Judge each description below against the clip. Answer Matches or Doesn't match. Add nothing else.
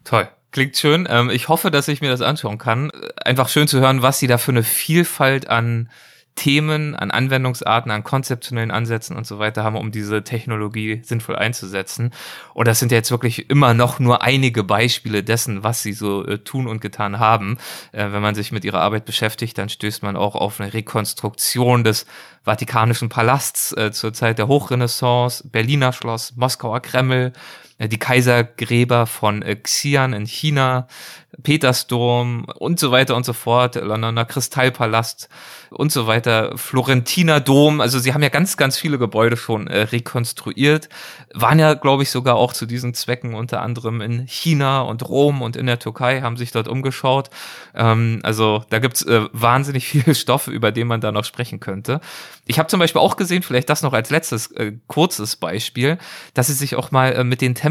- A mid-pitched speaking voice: Doesn't match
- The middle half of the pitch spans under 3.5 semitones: Matches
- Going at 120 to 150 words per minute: Doesn't match